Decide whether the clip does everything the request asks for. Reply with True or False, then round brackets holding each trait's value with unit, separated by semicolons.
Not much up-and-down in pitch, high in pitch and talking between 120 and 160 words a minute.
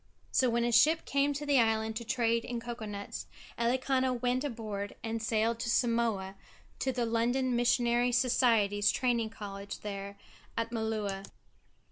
True (2.2 semitones; 235 Hz; 150 wpm)